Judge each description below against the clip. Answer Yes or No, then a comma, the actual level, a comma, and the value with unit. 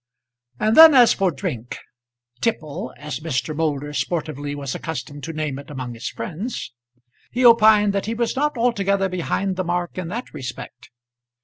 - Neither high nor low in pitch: Yes, medium, 170 Hz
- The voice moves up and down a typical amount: No, wide, 6.7 semitones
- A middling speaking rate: Yes, average, 165 wpm